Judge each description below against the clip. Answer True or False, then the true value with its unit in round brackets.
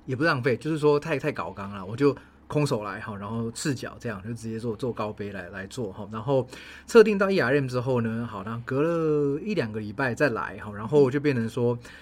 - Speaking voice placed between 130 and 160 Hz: False (120 Hz)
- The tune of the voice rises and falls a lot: False (4.8 semitones)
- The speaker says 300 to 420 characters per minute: True (330 characters per minute)